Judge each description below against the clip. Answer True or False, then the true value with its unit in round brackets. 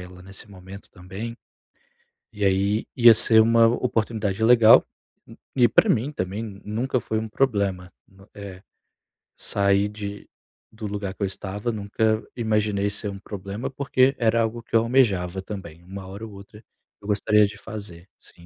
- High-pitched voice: False (105 Hz)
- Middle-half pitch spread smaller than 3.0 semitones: True (2.5 semitones)